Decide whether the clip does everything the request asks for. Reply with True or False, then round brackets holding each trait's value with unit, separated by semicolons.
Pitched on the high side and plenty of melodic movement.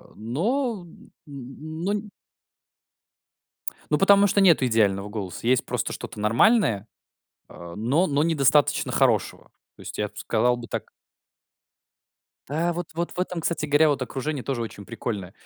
False (140 Hz; 7.2 semitones)